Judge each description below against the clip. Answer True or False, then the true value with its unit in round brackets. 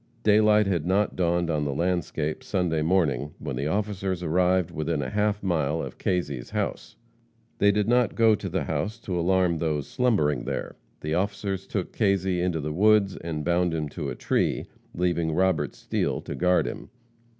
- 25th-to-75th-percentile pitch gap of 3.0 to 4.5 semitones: True (3.7 semitones)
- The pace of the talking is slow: False (175 wpm)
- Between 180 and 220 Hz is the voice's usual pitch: False (90 Hz)